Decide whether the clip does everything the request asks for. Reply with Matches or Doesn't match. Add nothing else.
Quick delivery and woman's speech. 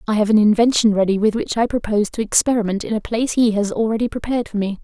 Matches